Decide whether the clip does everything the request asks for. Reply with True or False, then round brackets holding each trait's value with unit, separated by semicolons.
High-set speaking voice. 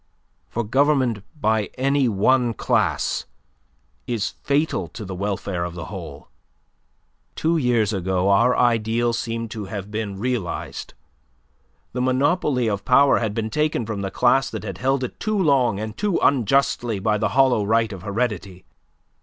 False (115 Hz)